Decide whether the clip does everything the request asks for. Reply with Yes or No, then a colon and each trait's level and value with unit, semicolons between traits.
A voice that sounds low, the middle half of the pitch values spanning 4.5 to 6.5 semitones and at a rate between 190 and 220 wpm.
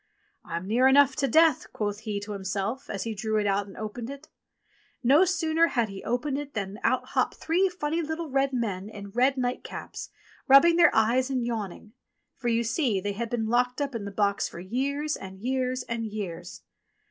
No: high, 240 Hz; average, 5.1 semitones; fast, 205 wpm